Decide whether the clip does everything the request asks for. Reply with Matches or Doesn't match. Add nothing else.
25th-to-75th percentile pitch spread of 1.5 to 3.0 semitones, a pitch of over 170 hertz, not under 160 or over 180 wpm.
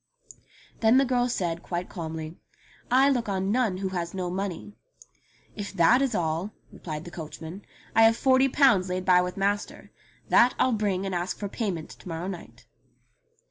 Doesn't match